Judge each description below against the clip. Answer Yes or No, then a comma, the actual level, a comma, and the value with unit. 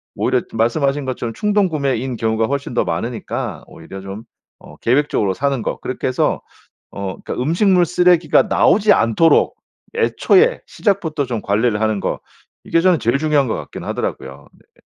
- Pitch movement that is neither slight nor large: No, wide, 6.8 semitones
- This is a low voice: Yes, low, 130 Hz